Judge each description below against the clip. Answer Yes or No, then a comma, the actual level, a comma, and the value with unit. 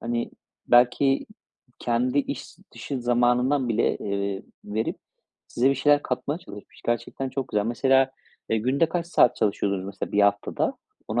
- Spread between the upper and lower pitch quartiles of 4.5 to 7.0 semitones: No, average, 3.8 semitones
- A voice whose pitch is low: Yes, low, 120 Hz